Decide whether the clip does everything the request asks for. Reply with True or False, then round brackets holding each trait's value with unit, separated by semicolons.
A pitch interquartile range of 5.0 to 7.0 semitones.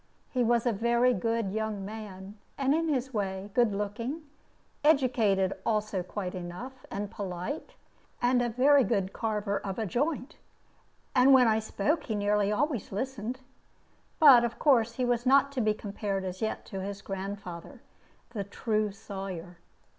False (4.1 semitones)